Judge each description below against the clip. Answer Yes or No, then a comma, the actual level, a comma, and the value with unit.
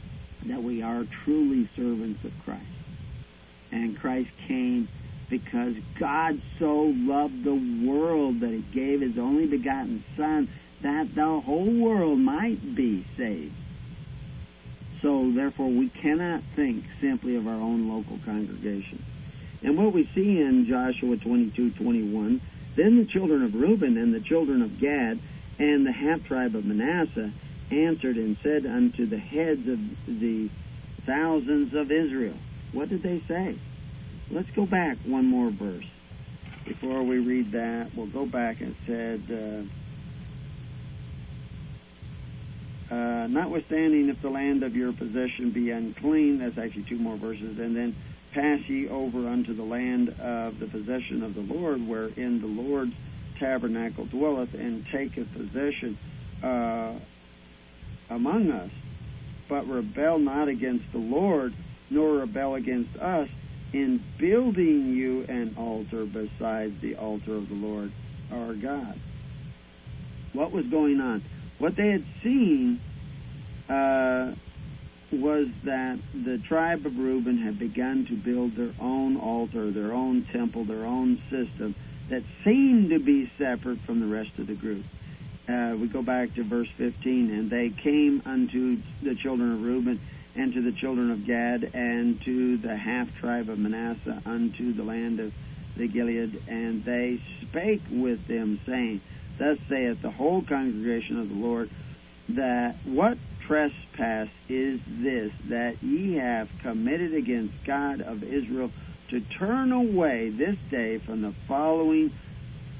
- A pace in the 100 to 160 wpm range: Yes, average, 140 wpm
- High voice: No, low, 125 Hz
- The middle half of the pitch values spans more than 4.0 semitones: Yes, average, 4.4 semitones